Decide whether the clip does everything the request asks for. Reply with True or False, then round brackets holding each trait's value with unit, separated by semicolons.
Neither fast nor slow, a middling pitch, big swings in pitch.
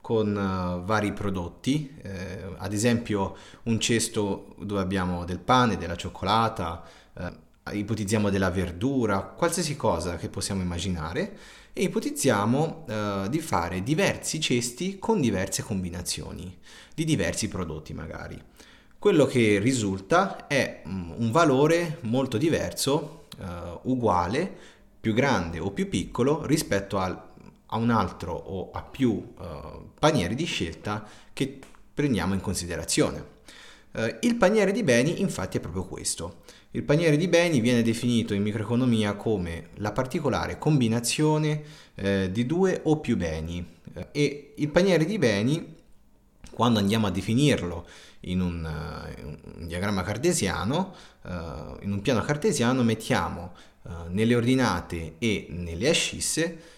False (130 wpm; 105 Hz; 6.3 semitones)